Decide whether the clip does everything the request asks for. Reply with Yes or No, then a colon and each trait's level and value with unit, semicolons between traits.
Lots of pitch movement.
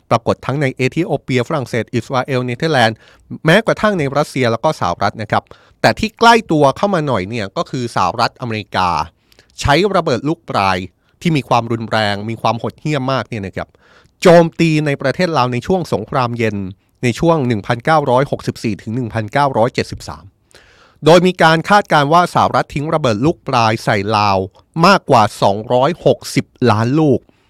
Yes: wide, 6.0 semitones